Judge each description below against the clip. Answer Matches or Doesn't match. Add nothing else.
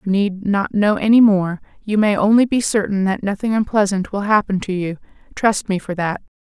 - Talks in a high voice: Matches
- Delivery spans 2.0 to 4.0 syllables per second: Doesn't match